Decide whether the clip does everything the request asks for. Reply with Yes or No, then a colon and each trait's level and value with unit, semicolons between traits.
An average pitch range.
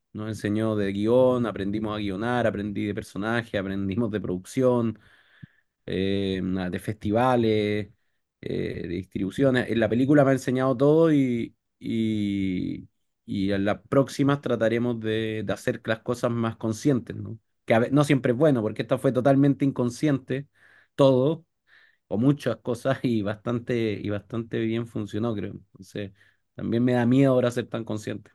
Yes: average, 3.5 semitones